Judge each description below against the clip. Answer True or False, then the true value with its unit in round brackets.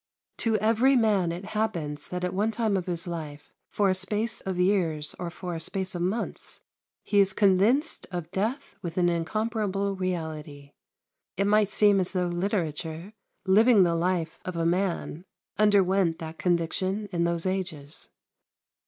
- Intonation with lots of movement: False (3.3 semitones)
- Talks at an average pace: True (160 wpm)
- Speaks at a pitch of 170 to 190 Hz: True (185 Hz)